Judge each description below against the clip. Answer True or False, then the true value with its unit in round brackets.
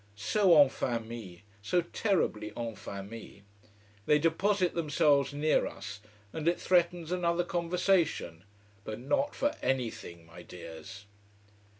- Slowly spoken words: True (115 wpm)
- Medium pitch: True (145 Hz)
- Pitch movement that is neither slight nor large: False (8.8 semitones)